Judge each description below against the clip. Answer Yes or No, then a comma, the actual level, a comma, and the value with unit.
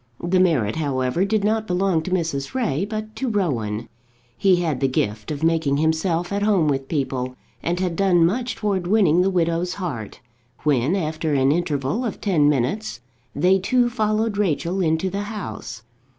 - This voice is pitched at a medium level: Yes, medium, 175 Hz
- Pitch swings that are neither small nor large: No, wide, 5.7 semitones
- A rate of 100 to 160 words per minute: No, average, 170 wpm